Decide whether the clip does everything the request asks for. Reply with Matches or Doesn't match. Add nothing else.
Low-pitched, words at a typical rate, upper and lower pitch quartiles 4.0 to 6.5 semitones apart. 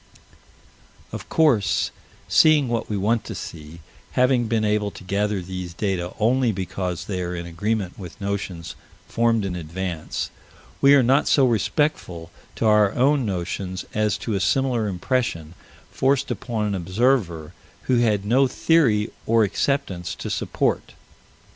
Matches